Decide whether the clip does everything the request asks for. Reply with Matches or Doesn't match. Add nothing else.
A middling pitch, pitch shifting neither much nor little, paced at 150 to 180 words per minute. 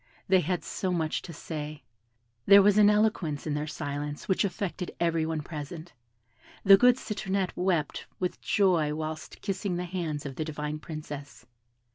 Matches